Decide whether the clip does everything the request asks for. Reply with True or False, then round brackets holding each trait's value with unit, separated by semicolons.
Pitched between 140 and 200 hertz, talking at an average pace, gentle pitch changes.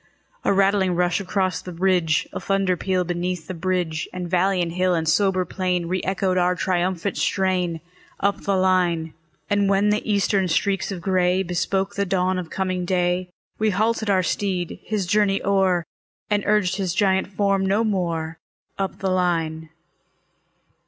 True (185 Hz; 165 wpm; 1.7 semitones)